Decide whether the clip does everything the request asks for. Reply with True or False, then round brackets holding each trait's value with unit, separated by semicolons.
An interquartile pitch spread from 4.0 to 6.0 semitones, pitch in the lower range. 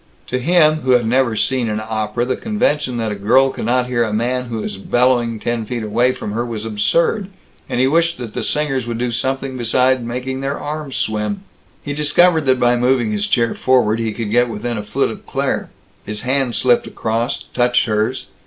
False (2.8 semitones; 120 Hz)